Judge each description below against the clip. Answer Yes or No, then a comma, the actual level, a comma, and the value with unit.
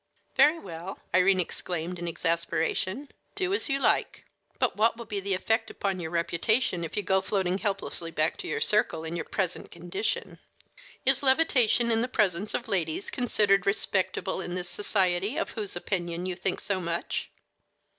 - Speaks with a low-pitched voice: No, high, 190 Hz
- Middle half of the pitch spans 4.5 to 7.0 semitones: No, average, 3.8 semitones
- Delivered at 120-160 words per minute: No, average, 170 wpm